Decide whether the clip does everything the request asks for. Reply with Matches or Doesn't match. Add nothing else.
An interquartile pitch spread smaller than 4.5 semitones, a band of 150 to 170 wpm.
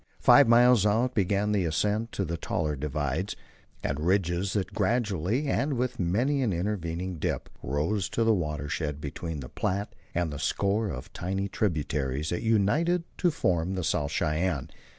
Doesn't match